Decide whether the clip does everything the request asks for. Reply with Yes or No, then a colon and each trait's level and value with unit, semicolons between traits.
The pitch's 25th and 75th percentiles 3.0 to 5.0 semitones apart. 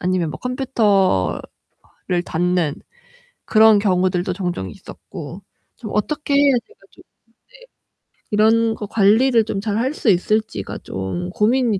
Yes: average, 4.2 semitones